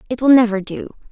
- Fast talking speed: Yes, fast, 215 wpm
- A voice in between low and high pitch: No, high, 230 Hz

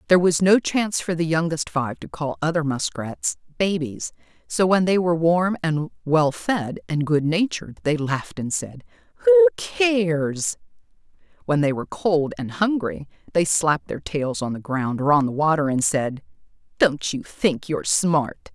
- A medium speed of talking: Yes, average, 170 wpm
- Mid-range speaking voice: Yes, medium, 155 Hz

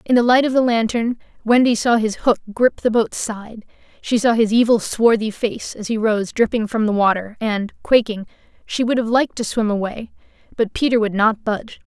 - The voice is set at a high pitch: Yes, high, 225 Hz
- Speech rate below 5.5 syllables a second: Yes, 5.2 syllables/s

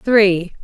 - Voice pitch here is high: Yes, high, 200 Hz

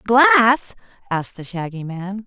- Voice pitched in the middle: No, high, 210 Hz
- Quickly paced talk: No, slow, 135 wpm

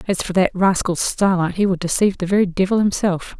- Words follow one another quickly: Yes, fast, 210 wpm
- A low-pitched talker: No, high, 190 Hz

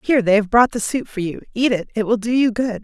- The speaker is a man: No, female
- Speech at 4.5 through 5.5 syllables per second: No, 6.3 syllables/s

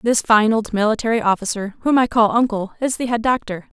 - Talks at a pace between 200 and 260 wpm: Yes, fast, 205 wpm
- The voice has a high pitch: Yes, high, 225 Hz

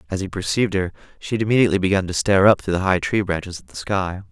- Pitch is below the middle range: Yes, very low, 95 Hz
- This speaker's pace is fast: Yes, fast, 265 wpm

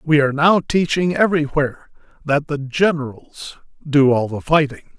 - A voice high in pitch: No, medium, 150 Hz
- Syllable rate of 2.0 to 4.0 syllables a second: No, 5.2 syllables/s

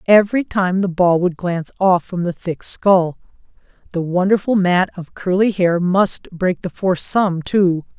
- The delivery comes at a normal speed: Yes, average, 175 wpm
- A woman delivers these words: Yes, female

